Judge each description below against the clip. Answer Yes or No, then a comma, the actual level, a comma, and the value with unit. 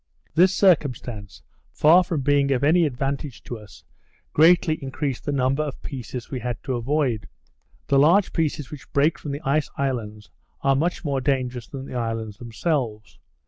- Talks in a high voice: No, low, 135 Hz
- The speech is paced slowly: No, average, 165 wpm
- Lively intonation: No, average, 3.7 semitones